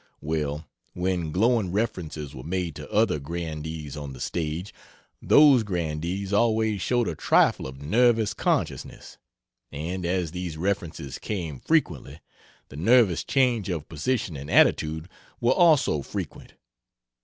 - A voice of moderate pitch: No, very low, 85 Hz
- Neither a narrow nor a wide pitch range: No, wide, 5.9 semitones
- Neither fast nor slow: No, slow, 130 wpm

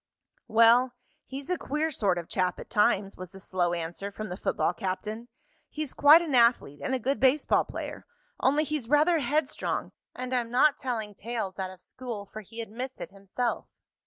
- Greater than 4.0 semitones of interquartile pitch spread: Yes, wide, 5.4 semitones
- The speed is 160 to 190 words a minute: Yes, average, 185 wpm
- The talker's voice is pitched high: Yes, high, 230 Hz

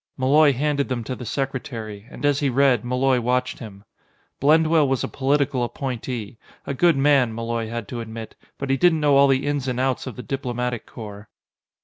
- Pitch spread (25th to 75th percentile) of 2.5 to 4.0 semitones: Yes, average, 2.9 semitones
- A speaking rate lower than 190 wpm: No, average, 195 wpm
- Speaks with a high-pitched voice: No, low, 130 Hz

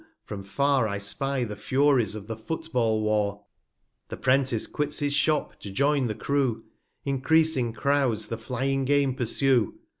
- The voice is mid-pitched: No, low, 130 Hz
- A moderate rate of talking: Yes, average, 160 wpm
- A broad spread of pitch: No, average, 4.4 semitones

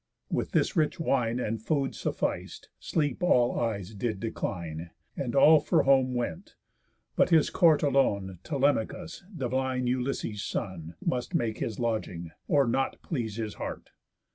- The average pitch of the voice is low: Yes, low, 125 Hz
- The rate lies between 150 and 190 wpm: No, average, 140 wpm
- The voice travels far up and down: No, average, 4.3 semitones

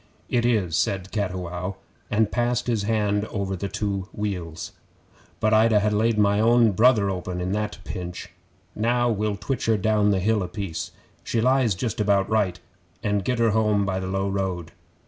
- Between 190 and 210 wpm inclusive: No, average, 180 wpm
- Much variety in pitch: No, narrow, 2.6 semitones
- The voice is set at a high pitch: No, low, 105 Hz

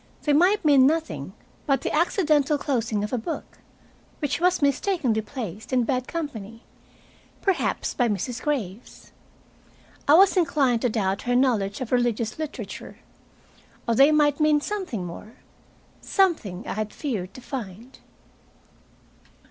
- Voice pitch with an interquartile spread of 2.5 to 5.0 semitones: No, wide, 5.6 semitones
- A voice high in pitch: Yes, very high, 255 Hz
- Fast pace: No, slow, 135 wpm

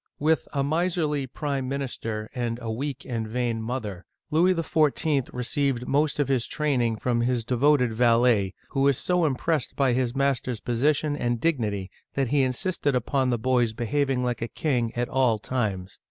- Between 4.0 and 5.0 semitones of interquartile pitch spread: No, average, 3.4 semitones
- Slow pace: No, average, 170 wpm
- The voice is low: Yes, low, 130 Hz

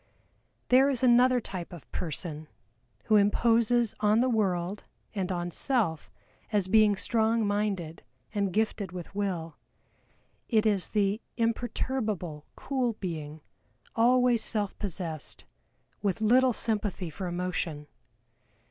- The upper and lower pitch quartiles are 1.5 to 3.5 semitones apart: No, average, 4.4 semitones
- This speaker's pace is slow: Yes, slow, 115 wpm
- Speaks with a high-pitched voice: Yes, high, 205 Hz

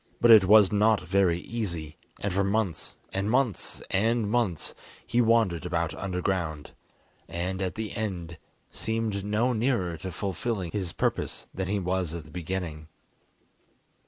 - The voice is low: Yes, very low, 95 Hz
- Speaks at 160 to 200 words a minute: No, average, 145 wpm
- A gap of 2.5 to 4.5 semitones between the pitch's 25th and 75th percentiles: Yes, average, 4.0 semitones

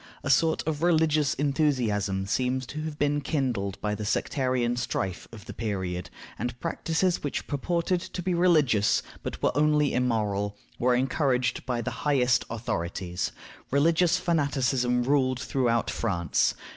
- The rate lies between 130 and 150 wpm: Yes, average, 140 wpm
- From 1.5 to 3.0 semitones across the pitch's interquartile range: No, average, 4.7 semitones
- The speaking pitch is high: No, low, 130 Hz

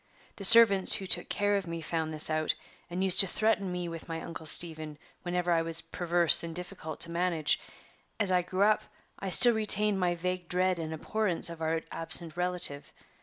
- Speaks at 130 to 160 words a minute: No, average, 195 wpm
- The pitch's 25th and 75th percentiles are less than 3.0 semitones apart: Yes, narrow, 2.6 semitones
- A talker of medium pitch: Yes, medium, 175 Hz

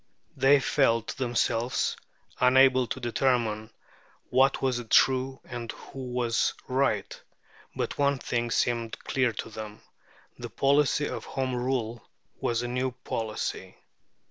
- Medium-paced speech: No, slow, 120 wpm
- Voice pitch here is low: Yes, low, 125 Hz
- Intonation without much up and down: Yes, narrow, 2.2 semitones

